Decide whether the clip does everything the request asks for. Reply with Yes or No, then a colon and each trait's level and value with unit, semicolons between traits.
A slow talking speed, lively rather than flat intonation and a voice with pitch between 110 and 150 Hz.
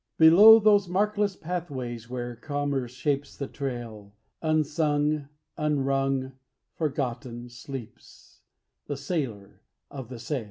No: slow, 105 wpm; average, 4.2 semitones; medium, 140 Hz